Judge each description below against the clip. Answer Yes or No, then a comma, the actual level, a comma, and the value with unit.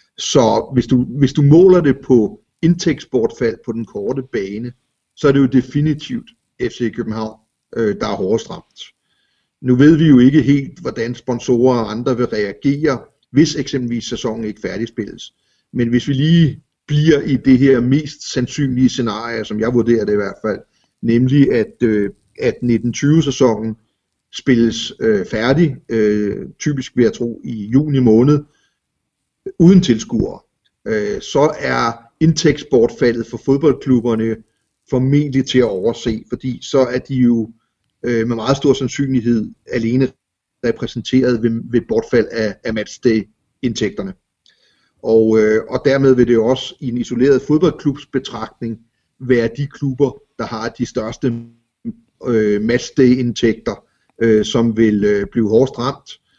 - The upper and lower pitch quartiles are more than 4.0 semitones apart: No, average, 3.3 semitones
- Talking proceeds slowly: Yes, slow, 130 wpm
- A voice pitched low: Yes, low, 125 Hz